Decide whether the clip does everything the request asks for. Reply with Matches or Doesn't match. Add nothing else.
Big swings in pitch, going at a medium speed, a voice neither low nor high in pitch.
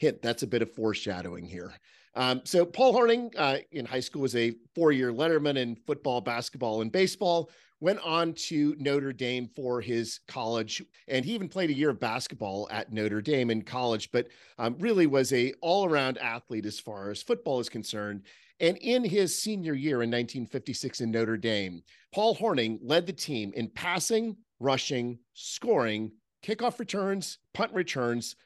Doesn't match